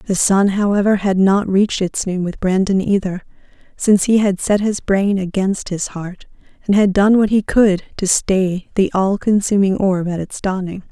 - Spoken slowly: No, average, 190 wpm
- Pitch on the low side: No, high, 195 Hz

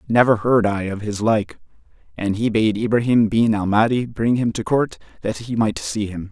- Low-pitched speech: Yes, low, 110 Hz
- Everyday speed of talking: No, fast, 210 wpm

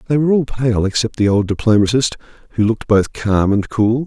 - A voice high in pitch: No, low, 115 Hz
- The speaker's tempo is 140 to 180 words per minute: No, fast, 205 wpm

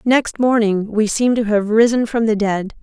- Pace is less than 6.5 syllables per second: Yes, 4.8 syllables/s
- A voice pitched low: No, high, 220 Hz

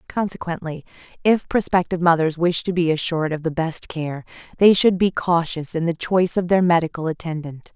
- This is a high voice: No, medium, 170 Hz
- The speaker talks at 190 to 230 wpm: No, average, 180 wpm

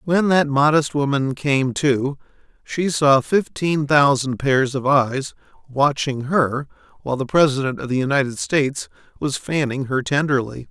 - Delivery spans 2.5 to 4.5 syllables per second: Yes, 4.4 syllables/s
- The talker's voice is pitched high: No, medium, 140 Hz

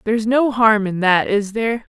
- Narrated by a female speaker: Yes, female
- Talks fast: Yes, fast, 215 wpm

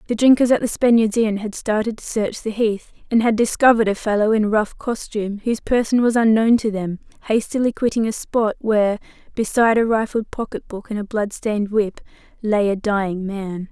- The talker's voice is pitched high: Yes, high, 215 Hz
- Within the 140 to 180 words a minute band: No, average, 195 wpm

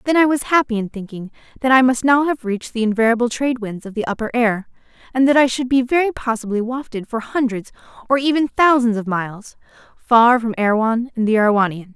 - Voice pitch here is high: Yes, high, 235 Hz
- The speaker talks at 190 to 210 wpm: Yes, fast, 205 wpm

